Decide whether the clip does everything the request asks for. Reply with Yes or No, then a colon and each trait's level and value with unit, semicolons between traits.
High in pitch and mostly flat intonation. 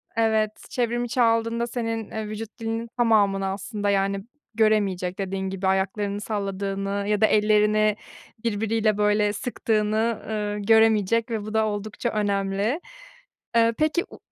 Yes: high, 215 Hz; narrow, 2.0 semitones